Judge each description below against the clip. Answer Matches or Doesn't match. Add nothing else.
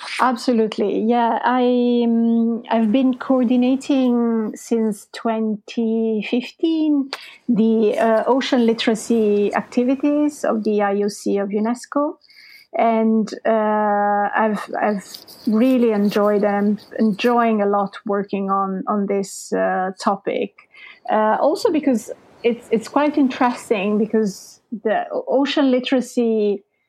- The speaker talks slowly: Matches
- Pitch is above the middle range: Matches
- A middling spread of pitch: Matches